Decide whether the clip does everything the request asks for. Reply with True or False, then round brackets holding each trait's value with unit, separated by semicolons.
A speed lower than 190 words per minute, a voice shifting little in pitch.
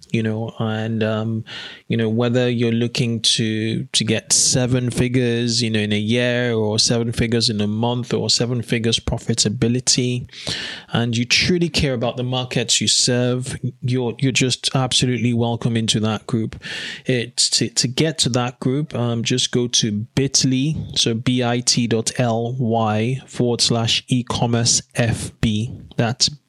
True (150 wpm; 1.8 semitones)